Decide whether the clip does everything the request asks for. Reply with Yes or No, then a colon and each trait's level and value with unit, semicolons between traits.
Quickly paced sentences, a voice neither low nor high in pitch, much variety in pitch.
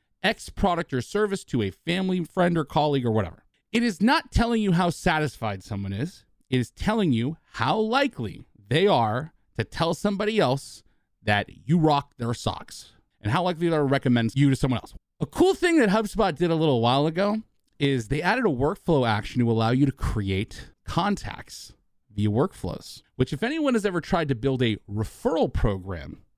No: average, 190 wpm; medium, 145 Hz; wide, 8.1 semitones